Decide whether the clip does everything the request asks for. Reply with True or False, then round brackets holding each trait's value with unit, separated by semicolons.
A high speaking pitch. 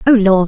True (205 Hz)